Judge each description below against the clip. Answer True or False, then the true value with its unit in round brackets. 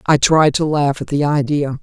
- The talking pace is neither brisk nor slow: False (230 wpm)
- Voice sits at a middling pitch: True (145 Hz)